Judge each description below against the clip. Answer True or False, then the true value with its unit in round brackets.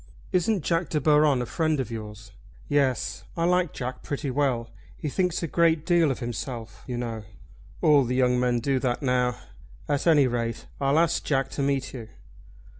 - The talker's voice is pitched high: False (135 Hz)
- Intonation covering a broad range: False (4.0 semitones)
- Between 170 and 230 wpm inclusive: True (185 wpm)